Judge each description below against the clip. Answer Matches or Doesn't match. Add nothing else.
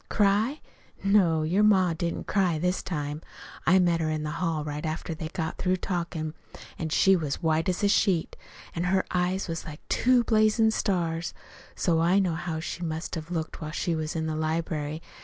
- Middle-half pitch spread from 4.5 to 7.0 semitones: Doesn't match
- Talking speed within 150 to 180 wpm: Doesn't match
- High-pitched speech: Doesn't match